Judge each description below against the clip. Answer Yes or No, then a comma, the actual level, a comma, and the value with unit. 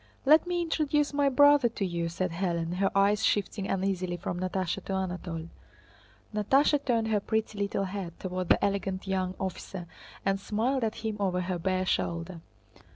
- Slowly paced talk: No, average, 165 wpm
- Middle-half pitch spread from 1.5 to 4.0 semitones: Yes, average, 3.4 semitones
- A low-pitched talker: No, high, 195 Hz